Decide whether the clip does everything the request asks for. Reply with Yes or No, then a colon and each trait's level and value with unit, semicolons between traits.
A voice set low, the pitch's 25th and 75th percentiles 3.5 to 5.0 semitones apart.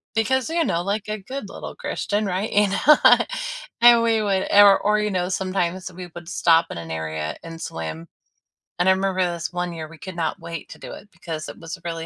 No: medium, 185 Hz; average, 3.8 semitones